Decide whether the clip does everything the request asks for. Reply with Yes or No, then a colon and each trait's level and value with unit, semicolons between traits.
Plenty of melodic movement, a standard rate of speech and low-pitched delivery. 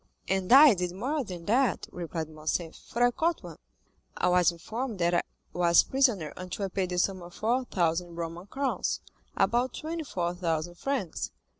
No: wide, 6.0 semitones; average, 155 wpm; medium, 185 Hz